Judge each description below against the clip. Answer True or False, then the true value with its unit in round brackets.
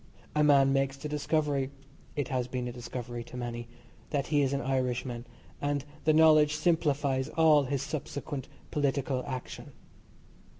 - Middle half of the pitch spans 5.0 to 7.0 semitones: False (2.7 semitones)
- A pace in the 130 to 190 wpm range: True (145 wpm)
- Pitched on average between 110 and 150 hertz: True (140 Hz)